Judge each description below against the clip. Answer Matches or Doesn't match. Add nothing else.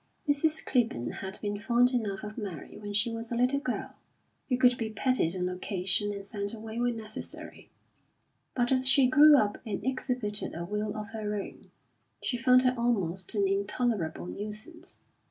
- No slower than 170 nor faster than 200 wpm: Matches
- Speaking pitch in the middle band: Doesn't match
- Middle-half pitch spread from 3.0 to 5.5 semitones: Matches